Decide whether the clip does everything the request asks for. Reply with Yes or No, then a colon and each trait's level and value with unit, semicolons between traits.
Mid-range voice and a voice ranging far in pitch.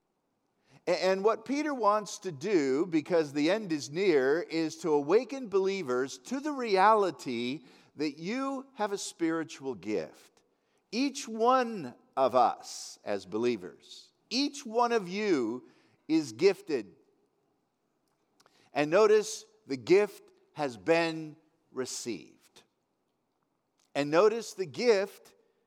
No: high, 210 Hz; wide, 9.0 semitones